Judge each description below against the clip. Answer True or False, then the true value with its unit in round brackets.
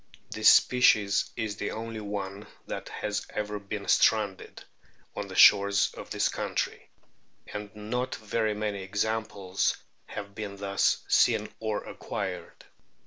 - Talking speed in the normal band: False (130 wpm)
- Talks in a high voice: False (105 Hz)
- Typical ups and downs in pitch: False (1.4 semitones)